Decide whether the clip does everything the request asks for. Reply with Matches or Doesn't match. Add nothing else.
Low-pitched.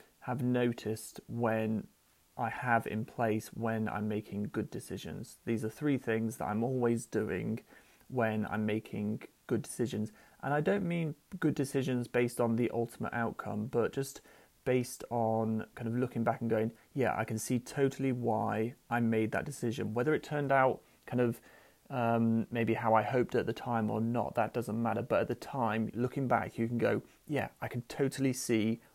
Matches